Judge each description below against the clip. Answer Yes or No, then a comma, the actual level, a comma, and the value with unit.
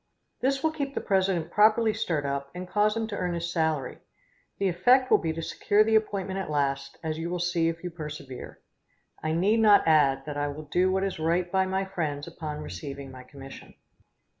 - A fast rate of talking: Yes, fast, 210 wpm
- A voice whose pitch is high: No, medium, 170 Hz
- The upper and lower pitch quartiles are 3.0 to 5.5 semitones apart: Yes, average, 4.6 semitones